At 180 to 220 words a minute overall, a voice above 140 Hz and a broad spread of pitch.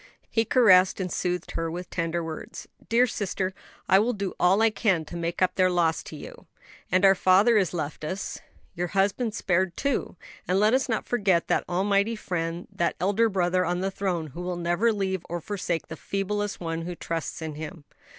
No: average, 200 wpm; medium, 185 Hz; average, 2.9 semitones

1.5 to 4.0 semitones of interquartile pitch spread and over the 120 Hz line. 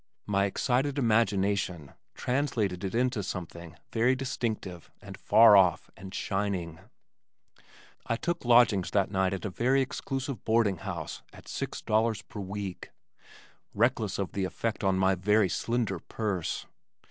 No: average, 3.7 semitones; low, 105 Hz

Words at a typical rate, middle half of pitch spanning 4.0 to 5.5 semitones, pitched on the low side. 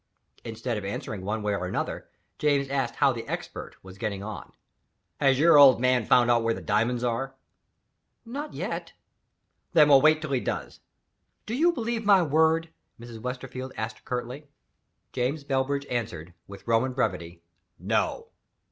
Yes: average, 155 wpm; average, 4.5 semitones; low, 125 Hz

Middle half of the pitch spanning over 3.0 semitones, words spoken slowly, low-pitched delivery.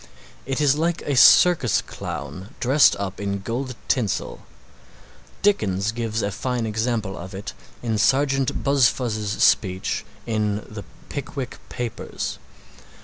Yes: average, 4.9 semitones; slow, 120 wpm; low, 115 Hz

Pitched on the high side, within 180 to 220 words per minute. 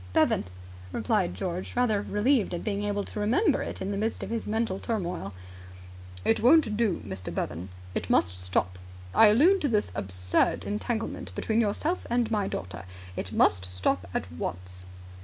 No: high, 205 Hz; average, 165 wpm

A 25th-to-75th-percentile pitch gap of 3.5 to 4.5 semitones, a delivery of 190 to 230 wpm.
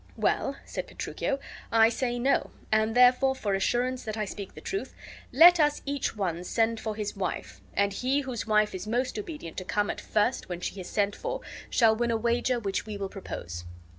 Yes: average, 4.0 semitones; average, 200 wpm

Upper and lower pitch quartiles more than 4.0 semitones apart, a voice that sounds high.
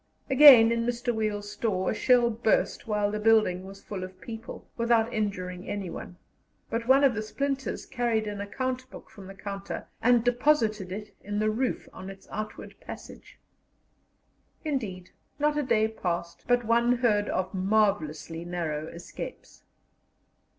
No: average, 3.6 semitones; high, 215 Hz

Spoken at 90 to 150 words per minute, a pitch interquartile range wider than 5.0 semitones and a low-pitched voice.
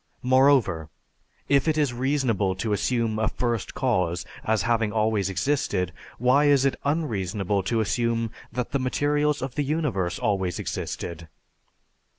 Yes: average, 140 wpm; wide, 5.4 semitones; low, 115 Hz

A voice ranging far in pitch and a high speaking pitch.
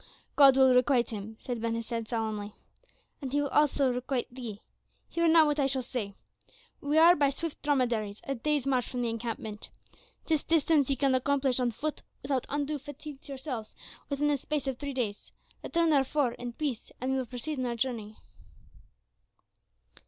No: average, 3.4 semitones; very high, 265 Hz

